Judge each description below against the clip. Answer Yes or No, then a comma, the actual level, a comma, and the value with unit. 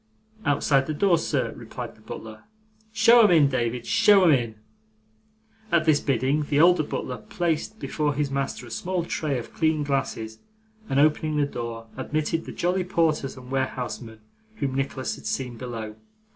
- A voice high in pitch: No, medium, 145 Hz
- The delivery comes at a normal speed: Yes, average, 165 wpm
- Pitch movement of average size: Yes, average, 4.4 semitones